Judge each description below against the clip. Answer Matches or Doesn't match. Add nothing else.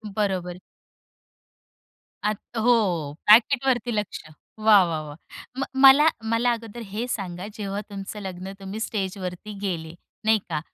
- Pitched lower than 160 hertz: Doesn't match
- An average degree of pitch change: Matches